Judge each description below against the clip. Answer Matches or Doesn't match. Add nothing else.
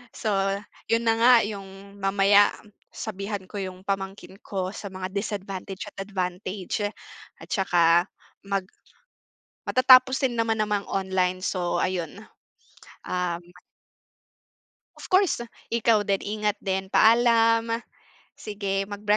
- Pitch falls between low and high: Doesn't match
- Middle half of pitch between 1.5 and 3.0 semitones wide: Matches